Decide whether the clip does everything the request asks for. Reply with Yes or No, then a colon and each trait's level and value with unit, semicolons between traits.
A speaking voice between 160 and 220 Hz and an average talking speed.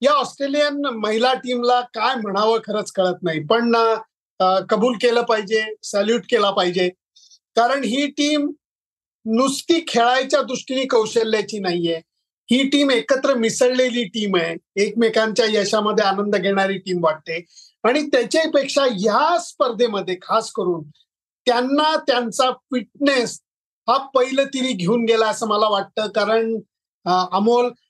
No: high, 230 Hz; average, 120 wpm